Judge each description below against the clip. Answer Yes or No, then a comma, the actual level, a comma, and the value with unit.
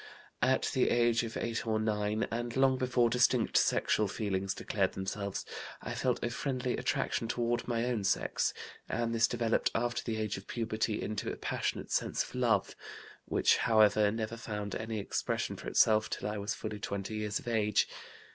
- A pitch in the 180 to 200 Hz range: No, low, 110 Hz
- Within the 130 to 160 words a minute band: No, average, 175 wpm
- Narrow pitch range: Yes, narrow, 2.1 semitones